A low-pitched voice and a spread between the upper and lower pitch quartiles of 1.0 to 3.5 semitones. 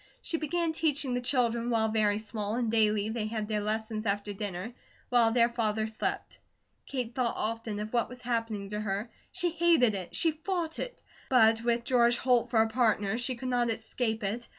No: high, 230 Hz; narrow, 2.5 semitones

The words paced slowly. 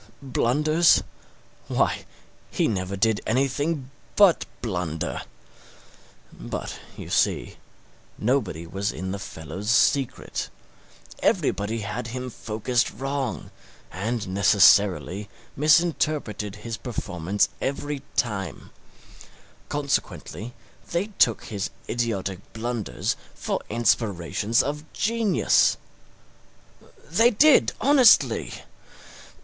Yes: slow, 85 wpm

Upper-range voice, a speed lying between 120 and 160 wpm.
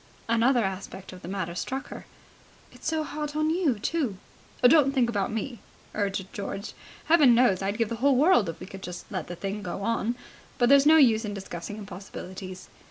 No: high, 220 Hz; average, 190 wpm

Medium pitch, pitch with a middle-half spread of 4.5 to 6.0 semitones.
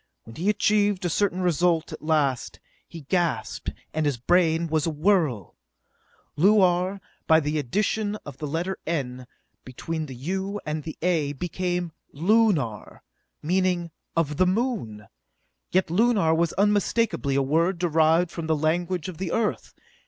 No: medium, 170 Hz; average, 3.7 semitones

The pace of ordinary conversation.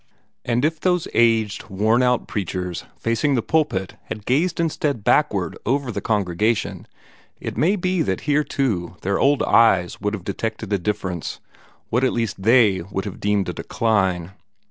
Yes: average, 165 wpm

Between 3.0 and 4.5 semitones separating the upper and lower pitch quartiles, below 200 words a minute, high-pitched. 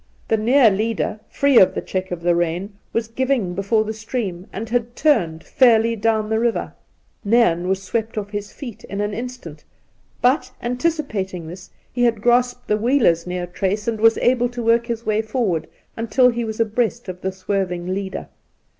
Yes: average, 3.9 semitones; average, 180 wpm; high, 220 Hz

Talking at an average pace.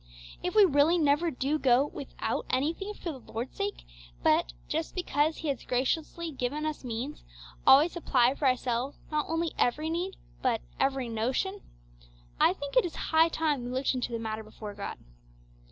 Yes: average, 170 wpm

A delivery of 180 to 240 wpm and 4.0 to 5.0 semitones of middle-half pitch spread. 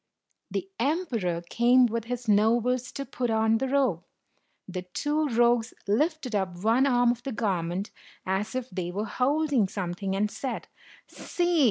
No: average, 155 wpm; average, 4.3 semitones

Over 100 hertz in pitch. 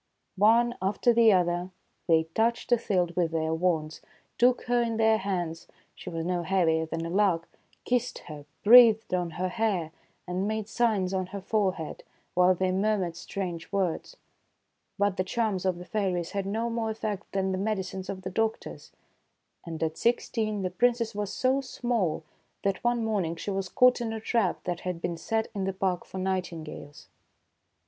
Yes: high, 190 Hz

